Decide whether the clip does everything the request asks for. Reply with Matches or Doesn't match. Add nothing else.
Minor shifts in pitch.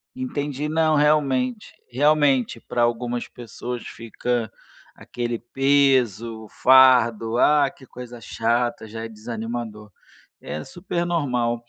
Doesn't match